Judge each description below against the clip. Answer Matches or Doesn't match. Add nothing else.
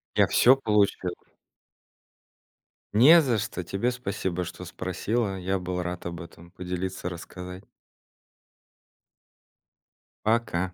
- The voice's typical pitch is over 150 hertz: Doesn't match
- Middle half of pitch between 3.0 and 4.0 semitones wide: Matches